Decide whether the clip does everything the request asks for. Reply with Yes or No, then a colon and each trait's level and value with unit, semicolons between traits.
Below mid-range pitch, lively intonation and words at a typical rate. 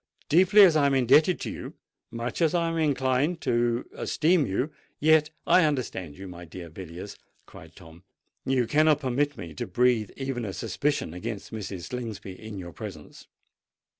Yes: low, 125 Hz; wide, 7.5 semitones; average, 165 wpm